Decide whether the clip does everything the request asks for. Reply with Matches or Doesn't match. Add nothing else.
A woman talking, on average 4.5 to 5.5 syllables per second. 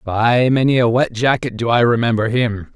Doesn't match